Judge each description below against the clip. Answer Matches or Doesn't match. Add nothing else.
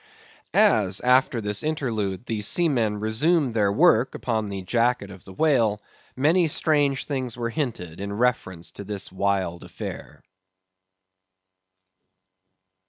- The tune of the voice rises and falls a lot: Doesn't match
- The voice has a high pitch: Doesn't match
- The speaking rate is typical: Doesn't match